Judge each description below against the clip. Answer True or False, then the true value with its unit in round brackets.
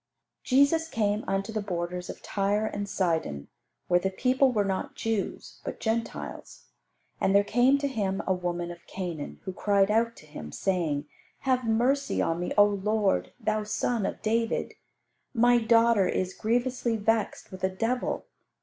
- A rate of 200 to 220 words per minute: False (160 wpm)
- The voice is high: True (205 Hz)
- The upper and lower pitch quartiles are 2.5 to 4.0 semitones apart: True (3.7 semitones)